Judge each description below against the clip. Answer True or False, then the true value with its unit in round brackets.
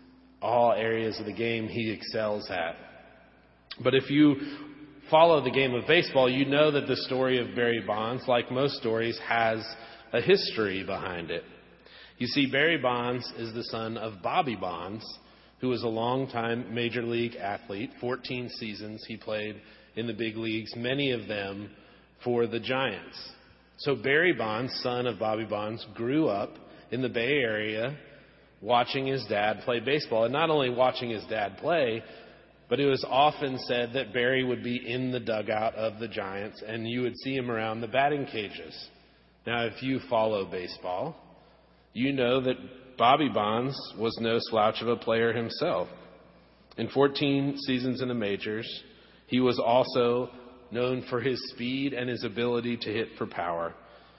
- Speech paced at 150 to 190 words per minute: True (165 wpm)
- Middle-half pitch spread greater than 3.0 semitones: False (2.5 semitones)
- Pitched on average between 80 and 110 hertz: False (120 Hz)